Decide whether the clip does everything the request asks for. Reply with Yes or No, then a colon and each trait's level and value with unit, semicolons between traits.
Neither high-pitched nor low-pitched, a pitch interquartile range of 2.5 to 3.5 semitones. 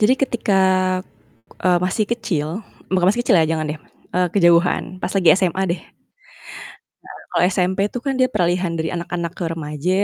Yes: medium, 180 Hz; average, 2.8 semitones